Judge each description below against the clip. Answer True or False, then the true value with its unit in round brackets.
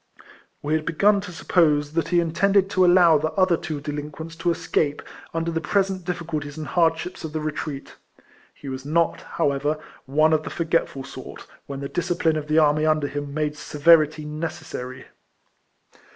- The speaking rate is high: False (170 wpm)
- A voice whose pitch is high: False (155 Hz)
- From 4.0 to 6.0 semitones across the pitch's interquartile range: False (2.4 semitones)